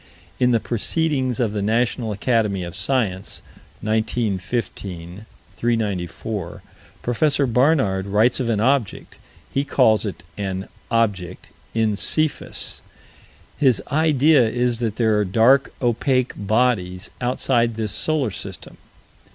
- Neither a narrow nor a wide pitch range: Yes, average, 3.7 semitones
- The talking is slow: Yes, slow, 115 wpm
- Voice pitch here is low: Yes, low, 115 Hz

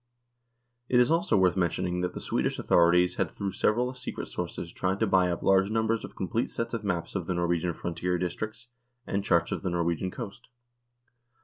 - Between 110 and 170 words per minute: No, average, 190 wpm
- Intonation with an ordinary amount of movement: Yes, average, 3.6 semitones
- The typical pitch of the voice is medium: No, very low, 95 Hz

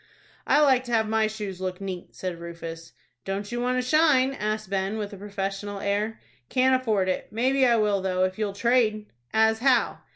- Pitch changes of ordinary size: Yes, average, 3.8 semitones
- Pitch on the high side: Yes, high, 215 Hz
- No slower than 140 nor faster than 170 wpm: No, average, 195 wpm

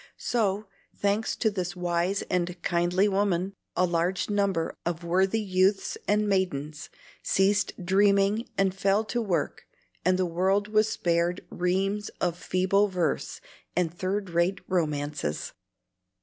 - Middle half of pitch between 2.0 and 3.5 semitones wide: Yes, narrow, 2.4 semitones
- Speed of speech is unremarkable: No, slow, 130 wpm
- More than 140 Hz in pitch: Yes, medium, 185 Hz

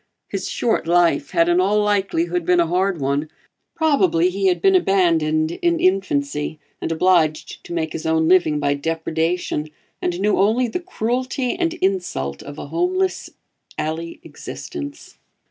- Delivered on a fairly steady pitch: No, average, 4.7 semitones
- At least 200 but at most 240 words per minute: No, average, 150 wpm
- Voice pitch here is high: No, medium, 175 Hz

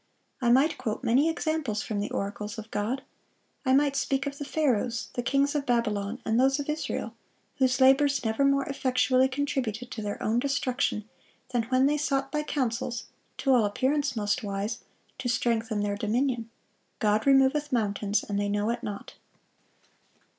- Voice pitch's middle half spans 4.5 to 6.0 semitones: No, average, 4.1 semitones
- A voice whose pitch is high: Yes, very high, 250 Hz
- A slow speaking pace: No, average, 170 wpm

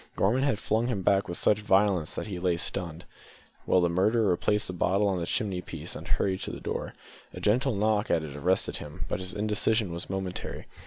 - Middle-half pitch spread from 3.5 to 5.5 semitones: No, average, 2.8 semitones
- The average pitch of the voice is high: No, very low, 95 Hz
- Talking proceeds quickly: Yes, fast, 215 wpm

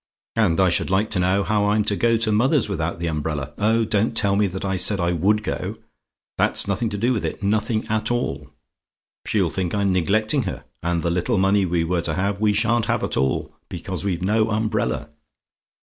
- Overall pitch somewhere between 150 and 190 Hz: No, low, 100 Hz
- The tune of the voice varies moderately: Yes, average, 3.5 semitones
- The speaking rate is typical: No, fast, 210 wpm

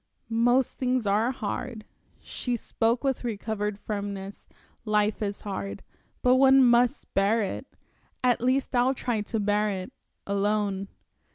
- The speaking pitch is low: No, high, 220 Hz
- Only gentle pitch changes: No, average, 3.4 semitones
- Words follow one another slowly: Yes, slow, 130 wpm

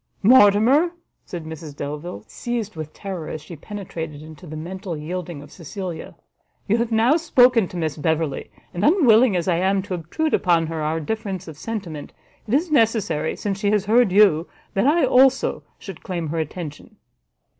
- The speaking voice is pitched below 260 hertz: Yes, medium, 185 Hz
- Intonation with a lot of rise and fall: Yes, wide, 5.8 semitones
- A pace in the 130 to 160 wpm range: No, average, 175 wpm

